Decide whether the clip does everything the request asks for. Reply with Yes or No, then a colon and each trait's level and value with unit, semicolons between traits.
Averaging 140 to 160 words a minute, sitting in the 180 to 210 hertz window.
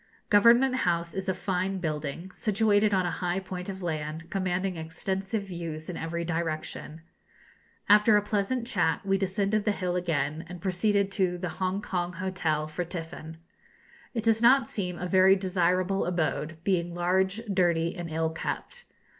Yes: average, 155 wpm; medium, 185 Hz